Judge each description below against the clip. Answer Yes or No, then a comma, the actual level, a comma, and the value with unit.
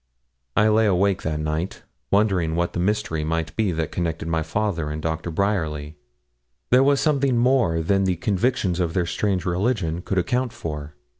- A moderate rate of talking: Yes, average, 170 wpm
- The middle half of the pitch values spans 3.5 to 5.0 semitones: Yes, average, 4.7 semitones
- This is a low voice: Yes, very low, 90 Hz